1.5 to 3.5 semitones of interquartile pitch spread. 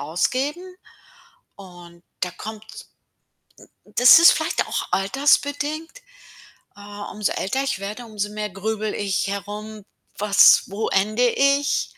No: average, 5.2 semitones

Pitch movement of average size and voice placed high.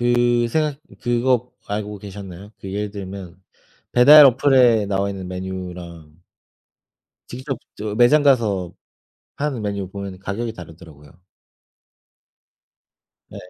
No: average, 4.5 semitones; low, 105 Hz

